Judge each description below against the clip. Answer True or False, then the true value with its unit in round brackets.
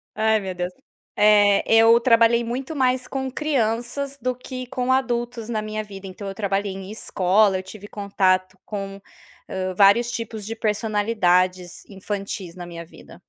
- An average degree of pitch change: True (3.5 semitones)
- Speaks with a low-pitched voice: False (215 Hz)